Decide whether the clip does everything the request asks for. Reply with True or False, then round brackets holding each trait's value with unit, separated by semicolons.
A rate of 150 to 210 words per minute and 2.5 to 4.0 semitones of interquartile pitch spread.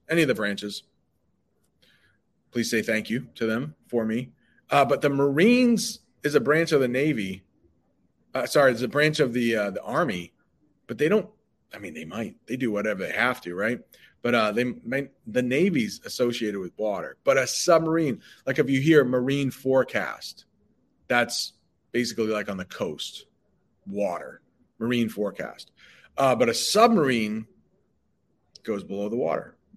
False (165 wpm; 5.3 semitones)